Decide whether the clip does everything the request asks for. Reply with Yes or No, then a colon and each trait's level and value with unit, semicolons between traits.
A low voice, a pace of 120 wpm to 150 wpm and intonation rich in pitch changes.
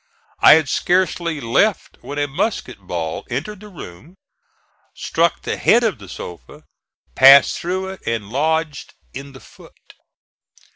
No: medium, 145 Hz; average, 140 wpm; wide, 6.6 semitones